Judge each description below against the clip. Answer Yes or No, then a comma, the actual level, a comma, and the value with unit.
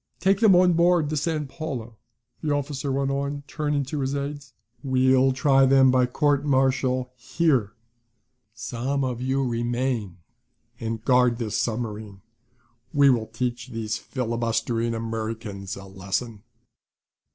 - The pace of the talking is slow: Yes, slow, 130 wpm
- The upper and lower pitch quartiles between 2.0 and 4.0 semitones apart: Yes, average, 3.5 semitones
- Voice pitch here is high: No, low, 130 Hz